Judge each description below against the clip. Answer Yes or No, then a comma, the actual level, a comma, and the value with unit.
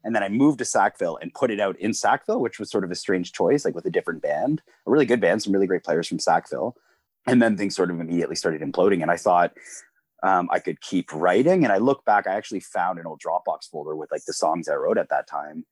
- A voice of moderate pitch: No, low, 120 Hz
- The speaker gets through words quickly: Yes, fast, 265 wpm